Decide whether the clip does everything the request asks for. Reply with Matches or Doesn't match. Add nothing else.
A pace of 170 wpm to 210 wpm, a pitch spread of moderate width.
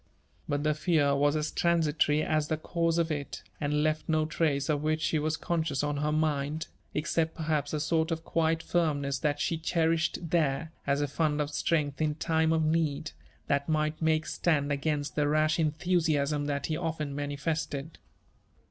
Doesn't match